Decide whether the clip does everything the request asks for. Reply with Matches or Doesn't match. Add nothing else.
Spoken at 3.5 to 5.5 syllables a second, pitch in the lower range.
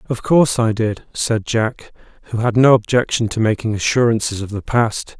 Matches